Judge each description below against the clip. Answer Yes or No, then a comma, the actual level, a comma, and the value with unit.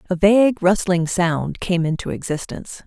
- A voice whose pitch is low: No, medium, 185 Hz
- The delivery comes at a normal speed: Yes, average, 145 wpm